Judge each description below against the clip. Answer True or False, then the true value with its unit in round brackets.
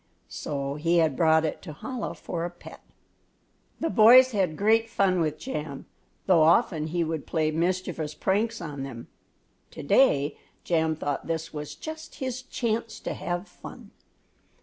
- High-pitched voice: False (170 Hz)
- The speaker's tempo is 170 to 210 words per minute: False (155 wpm)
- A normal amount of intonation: False (5.8 semitones)